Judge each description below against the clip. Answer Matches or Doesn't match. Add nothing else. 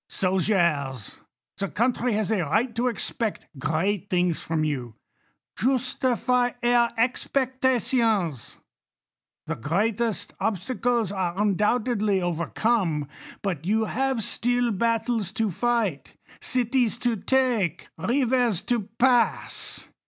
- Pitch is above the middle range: Matches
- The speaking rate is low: Matches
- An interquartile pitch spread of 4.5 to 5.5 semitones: Matches